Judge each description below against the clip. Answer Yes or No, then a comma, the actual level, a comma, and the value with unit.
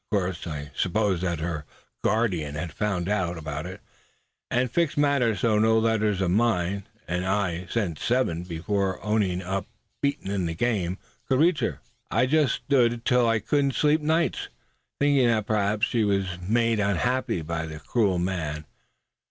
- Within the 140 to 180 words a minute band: Yes, average, 170 wpm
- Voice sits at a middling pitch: No, low, 100 Hz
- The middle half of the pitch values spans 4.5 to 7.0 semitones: Yes, average, 5.1 semitones